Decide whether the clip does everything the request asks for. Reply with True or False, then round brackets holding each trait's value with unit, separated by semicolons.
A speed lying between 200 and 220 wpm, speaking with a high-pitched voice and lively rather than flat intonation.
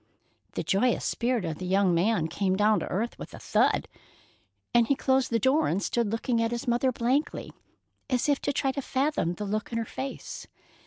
False (205 wpm; 235 Hz; 4.5 semitones)